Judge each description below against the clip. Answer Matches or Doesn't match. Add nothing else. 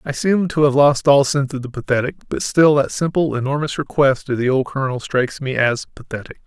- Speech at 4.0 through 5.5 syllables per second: Doesn't match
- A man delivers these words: Matches